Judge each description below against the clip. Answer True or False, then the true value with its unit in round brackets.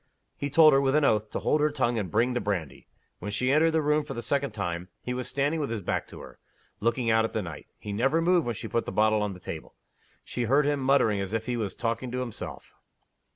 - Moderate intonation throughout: True (4.9 semitones)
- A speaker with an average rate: False (260 wpm)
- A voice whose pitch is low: True (120 Hz)